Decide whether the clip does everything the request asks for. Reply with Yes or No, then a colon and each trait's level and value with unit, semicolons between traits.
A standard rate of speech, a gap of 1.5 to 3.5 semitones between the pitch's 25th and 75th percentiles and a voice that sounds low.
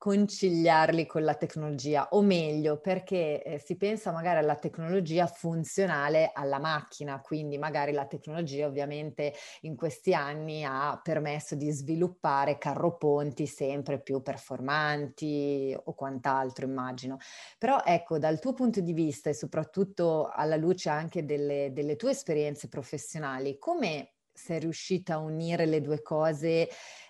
No: average, 135 wpm; narrow, 2.4 semitones; medium, 155 Hz